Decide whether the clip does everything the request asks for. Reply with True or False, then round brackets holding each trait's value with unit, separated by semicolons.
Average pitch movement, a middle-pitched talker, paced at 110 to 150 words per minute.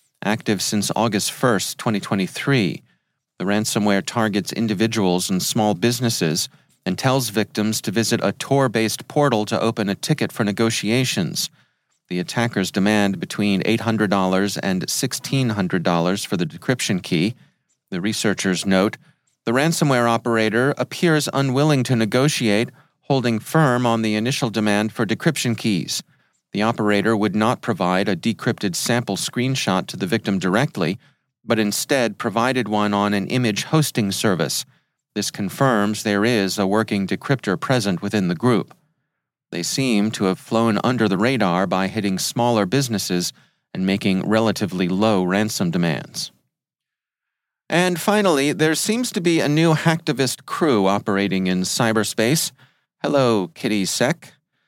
False (4.3 semitones; 110 Hz; 135 wpm)